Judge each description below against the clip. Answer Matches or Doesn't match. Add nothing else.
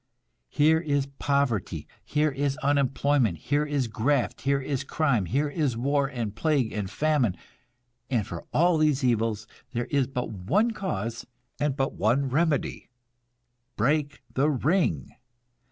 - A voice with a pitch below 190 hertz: Matches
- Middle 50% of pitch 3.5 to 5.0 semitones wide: Matches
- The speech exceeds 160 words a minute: Doesn't match